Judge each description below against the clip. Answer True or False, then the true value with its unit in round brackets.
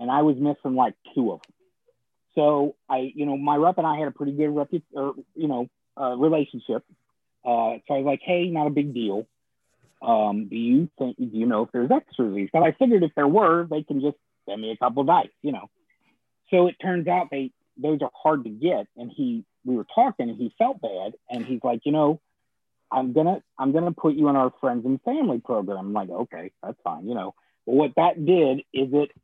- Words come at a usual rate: False (235 wpm)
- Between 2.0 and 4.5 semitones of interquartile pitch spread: True (4.0 semitones)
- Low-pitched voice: False (145 Hz)